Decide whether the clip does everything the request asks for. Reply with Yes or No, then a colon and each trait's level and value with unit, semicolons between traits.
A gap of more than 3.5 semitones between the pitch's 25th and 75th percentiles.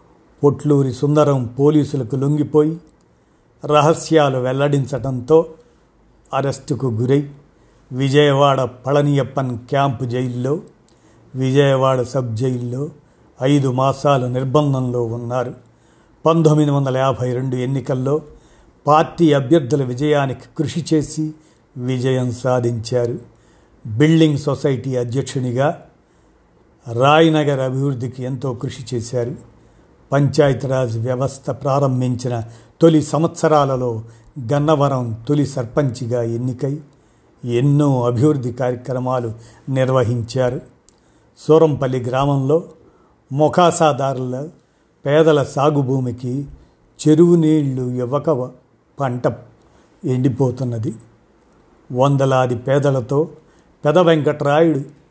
No: average, 2.8 semitones